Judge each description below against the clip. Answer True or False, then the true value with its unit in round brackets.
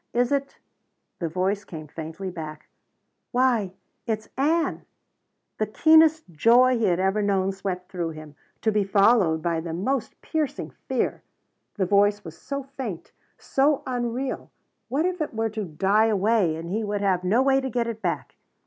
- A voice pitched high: True (210 Hz)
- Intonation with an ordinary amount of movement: False (5.8 semitones)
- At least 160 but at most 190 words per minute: True (170 wpm)